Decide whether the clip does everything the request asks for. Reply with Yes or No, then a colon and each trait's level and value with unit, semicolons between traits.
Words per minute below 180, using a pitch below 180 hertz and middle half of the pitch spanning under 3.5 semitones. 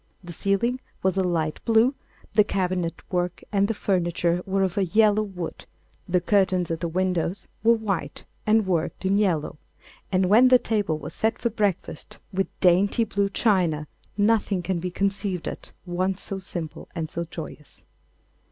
No: average, 165 wpm; high, 190 Hz; average, 2.9 semitones